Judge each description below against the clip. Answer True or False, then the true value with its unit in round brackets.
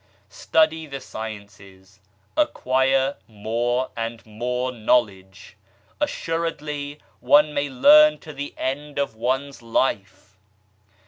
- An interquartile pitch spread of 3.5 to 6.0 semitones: True (4.7 semitones)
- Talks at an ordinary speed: False (95 wpm)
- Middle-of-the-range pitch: False (130 Hz)